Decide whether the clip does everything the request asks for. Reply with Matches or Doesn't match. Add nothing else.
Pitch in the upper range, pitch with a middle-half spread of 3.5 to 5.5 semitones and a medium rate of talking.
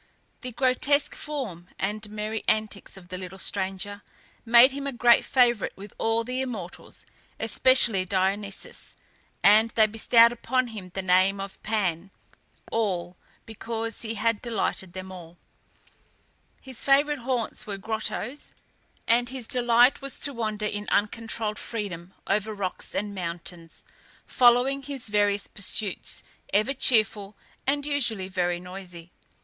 Doesn't match